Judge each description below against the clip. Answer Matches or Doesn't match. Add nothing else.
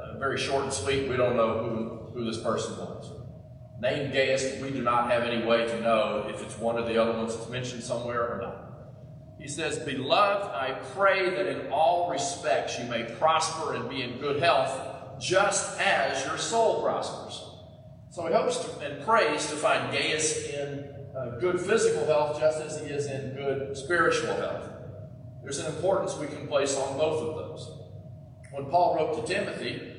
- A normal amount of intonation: Matches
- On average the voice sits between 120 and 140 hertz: Matches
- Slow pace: Doesn't match